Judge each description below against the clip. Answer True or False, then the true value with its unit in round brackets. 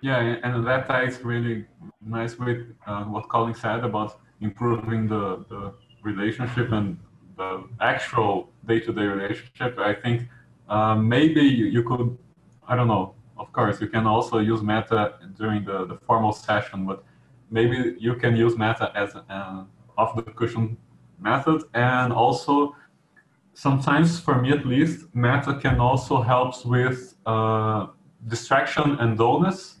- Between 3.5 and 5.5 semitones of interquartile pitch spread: False (2.7 semitones)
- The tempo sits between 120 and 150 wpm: True (135 wpm)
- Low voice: True (115 Hz)